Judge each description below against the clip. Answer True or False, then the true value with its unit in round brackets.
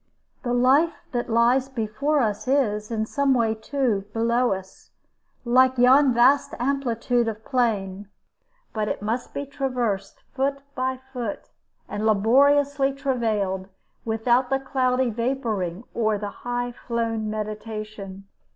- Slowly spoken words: True (125 wpm)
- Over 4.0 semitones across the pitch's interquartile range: False (3.5 semitones)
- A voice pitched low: False (240 Hz)